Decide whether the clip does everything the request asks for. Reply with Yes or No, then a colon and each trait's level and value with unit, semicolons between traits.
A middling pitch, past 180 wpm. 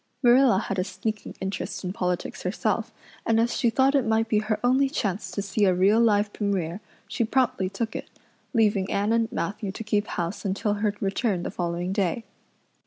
No: high, 210 Hz; average, 190 wpm